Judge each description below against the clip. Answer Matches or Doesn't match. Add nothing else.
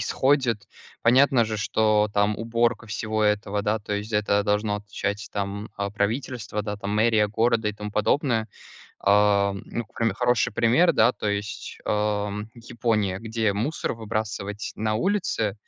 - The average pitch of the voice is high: Doesn't match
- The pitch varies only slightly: Matches